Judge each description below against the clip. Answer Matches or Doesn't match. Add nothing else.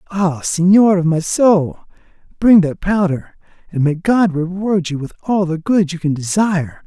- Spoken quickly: Doesn't match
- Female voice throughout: Doesn't match